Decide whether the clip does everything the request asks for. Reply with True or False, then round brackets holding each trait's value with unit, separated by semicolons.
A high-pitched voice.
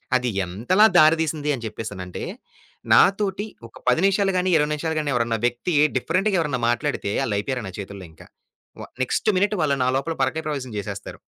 False (140 Hz)